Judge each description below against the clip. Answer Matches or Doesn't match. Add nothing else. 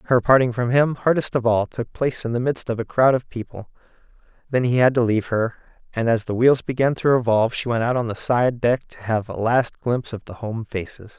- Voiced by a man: Matches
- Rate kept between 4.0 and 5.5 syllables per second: Doesn't match